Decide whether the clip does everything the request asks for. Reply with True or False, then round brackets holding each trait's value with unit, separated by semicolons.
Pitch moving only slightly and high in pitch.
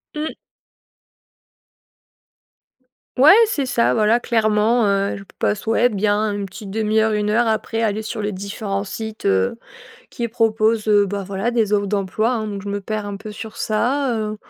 True (1.8 semitones; 215 Hz)